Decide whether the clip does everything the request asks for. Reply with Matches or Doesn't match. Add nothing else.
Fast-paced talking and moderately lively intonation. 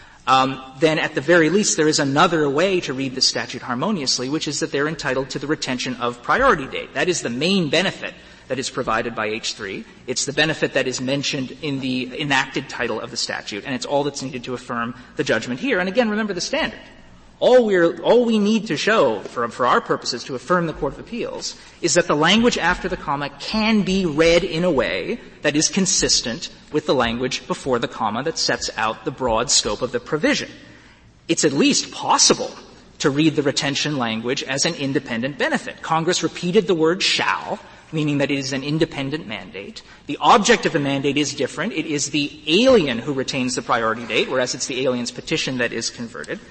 Matches